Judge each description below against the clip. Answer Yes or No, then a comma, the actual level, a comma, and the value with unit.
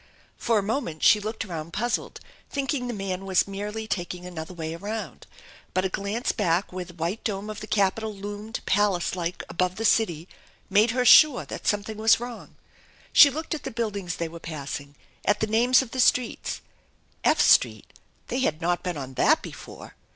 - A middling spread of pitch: Yes, average, 4.1 semitones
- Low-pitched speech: No, high, 205 Hz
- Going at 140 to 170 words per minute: No, average, 190 wpm